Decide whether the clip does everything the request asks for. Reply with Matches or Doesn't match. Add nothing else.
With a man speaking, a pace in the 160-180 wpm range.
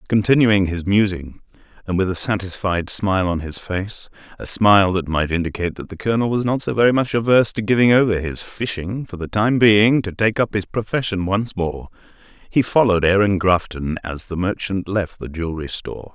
Doesn't match